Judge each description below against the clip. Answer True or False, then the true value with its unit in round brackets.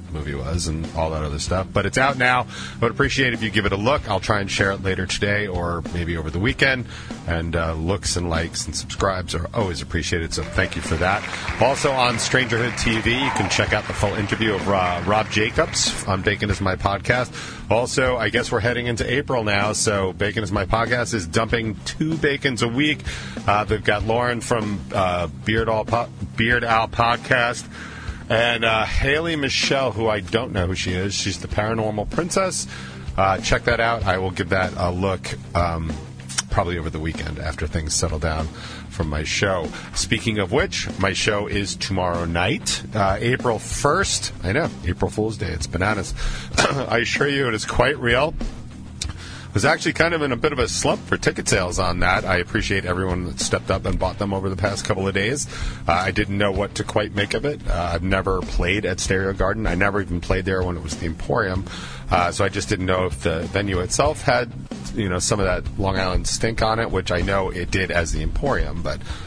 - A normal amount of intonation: True (4.2 semitones)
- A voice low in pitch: True (100 Hz)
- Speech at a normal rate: False (215 wpm)